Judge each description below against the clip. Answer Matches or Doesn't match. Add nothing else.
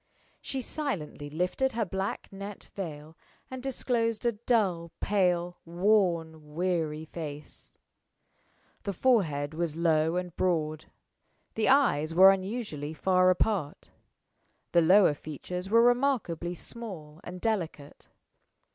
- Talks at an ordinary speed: Doesn't match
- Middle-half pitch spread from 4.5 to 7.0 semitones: Matches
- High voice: Doesn't match